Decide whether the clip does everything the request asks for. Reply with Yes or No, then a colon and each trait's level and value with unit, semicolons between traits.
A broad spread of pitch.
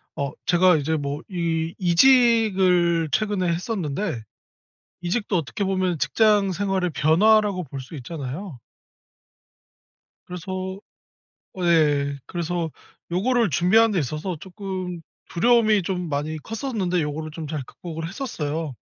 No: average, 4.0 semitones